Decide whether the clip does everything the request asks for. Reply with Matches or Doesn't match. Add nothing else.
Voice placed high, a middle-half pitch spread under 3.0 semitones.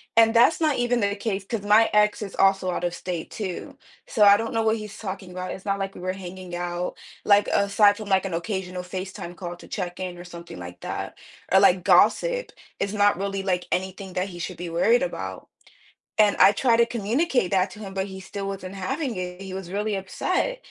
Matches